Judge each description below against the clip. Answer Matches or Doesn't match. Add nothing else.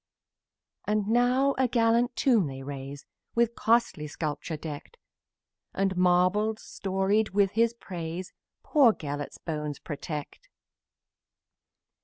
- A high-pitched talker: Matches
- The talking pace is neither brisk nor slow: Doesn't match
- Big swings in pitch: Matches